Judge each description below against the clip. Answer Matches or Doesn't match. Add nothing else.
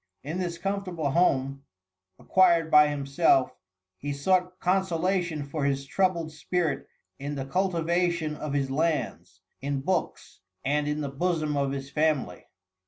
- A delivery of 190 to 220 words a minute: Doesn't match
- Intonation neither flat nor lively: Matches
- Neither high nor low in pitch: Matches